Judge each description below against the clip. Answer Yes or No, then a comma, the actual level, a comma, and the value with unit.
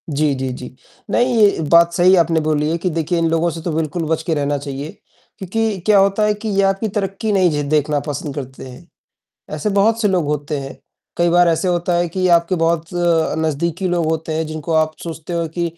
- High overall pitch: No, medium, 165 Hz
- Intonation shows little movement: No, average, 3.3 semitones